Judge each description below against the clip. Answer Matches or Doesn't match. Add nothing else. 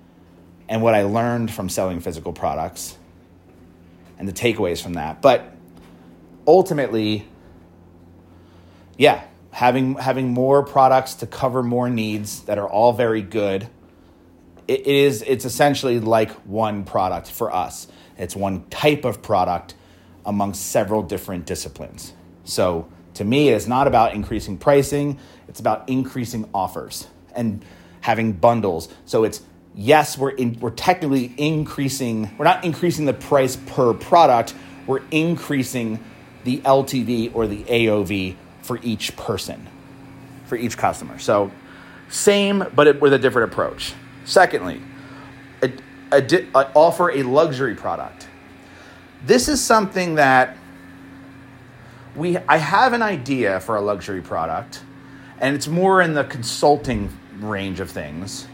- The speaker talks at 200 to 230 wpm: Doesn't match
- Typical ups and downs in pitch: Doesn't match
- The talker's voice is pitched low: Matches